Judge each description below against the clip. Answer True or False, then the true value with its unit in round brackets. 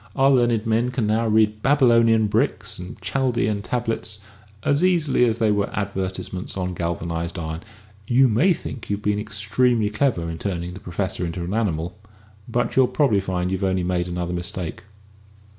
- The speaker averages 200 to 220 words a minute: False (170 wpm)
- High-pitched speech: False (105 Hz)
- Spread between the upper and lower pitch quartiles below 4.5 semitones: False (4.8 semitones)